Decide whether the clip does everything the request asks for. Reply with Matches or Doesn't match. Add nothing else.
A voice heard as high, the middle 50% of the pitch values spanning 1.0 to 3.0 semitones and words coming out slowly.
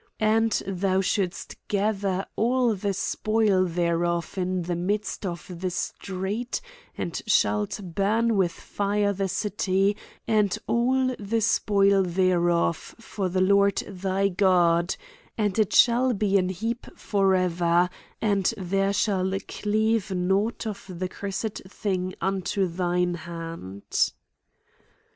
Matches